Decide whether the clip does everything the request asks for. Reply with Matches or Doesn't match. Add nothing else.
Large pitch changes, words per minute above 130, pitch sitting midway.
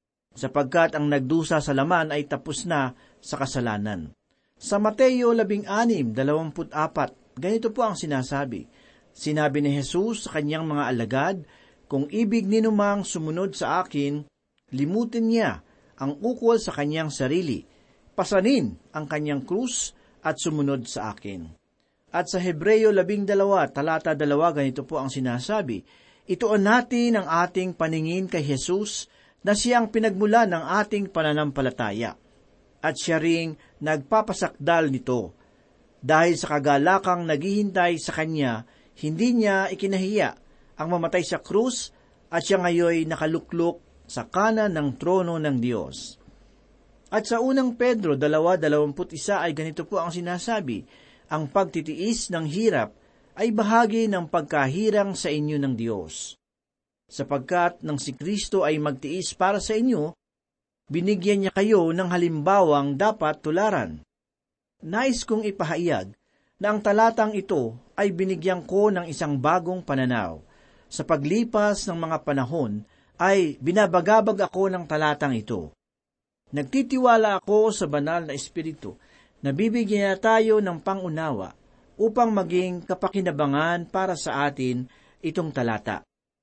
Doesn't match